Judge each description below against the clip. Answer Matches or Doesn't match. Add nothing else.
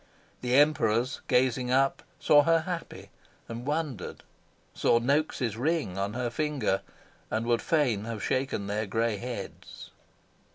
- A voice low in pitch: Matches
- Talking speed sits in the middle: Doesn't match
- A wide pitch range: Doesn't match